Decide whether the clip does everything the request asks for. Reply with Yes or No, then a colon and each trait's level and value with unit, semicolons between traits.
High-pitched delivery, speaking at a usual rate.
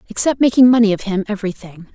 Yes: high, 215 Hz; average, 155 wpm